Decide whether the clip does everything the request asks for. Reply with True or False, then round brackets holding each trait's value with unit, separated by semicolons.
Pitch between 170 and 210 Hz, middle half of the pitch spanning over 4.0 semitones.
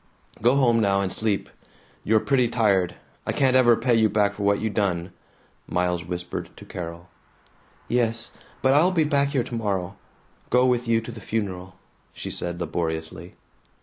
False (110 Hz; 5.0 semitones)